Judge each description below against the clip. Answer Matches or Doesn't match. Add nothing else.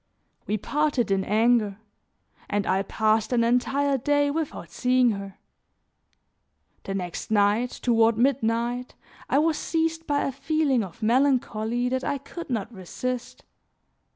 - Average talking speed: Doesn't match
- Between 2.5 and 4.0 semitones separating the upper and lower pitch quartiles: Doesn't match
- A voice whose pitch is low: Doesn't match